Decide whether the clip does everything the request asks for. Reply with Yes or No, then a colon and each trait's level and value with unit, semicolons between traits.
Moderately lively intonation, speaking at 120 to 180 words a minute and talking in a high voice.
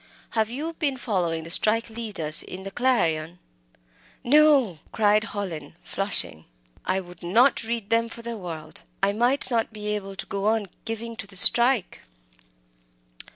Yes: average, 4.2 semitones; average, 155 wpm; high, 210 Hz